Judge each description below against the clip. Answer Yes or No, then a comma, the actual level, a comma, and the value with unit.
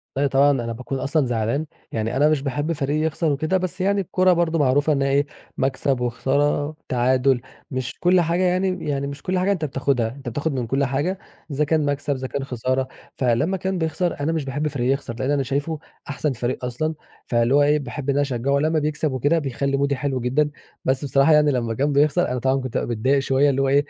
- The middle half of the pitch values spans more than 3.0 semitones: No, average, 2.7 semitones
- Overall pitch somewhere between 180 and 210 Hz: No, medium, 140 Hz